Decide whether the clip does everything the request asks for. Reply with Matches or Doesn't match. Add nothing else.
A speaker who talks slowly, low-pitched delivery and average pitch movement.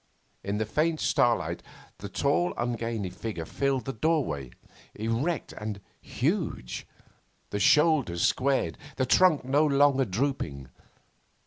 Doesn't match